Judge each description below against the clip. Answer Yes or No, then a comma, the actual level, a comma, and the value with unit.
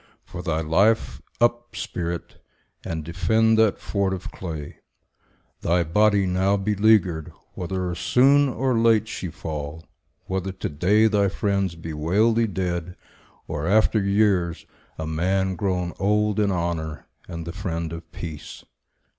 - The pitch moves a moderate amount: Yes, average, 4.0 semitones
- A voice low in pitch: Yes, very low, 95 Hz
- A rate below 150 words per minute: Yes, slow, 135 wpm